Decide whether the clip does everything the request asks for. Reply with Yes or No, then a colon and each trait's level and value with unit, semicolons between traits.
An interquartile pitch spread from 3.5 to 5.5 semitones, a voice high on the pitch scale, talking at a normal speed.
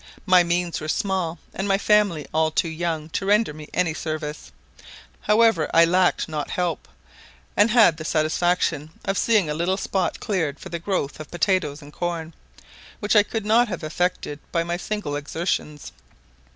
No: average, 3.9 semitones; medium, 175 Hz; average, 170 wpm